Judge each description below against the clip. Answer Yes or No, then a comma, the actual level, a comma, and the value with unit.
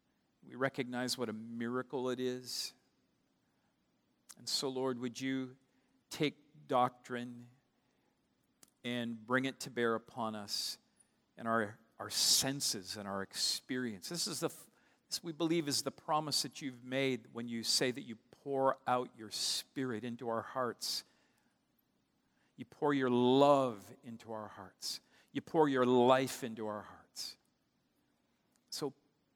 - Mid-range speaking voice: No, low, 125 Hz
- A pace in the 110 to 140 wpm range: Yes, slow, 135 wpm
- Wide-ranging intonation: No, average, 2.7 semitones